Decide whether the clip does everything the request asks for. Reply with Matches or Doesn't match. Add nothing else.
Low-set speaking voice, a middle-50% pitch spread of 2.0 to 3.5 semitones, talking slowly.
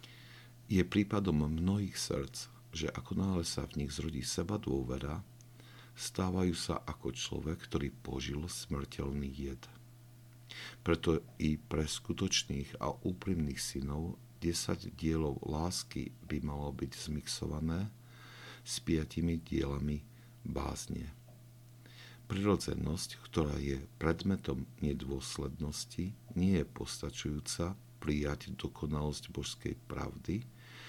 Doesn't match